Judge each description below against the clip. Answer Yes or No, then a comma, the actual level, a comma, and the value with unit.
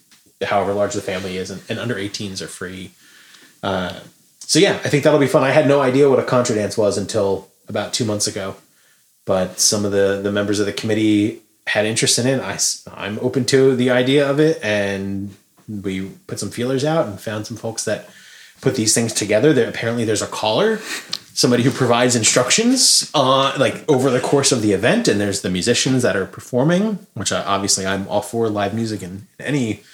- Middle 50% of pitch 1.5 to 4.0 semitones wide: No, average, 5.0 semitones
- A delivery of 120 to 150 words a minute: No, fast, 205 wpm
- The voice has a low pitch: Yes, low, 110 Hz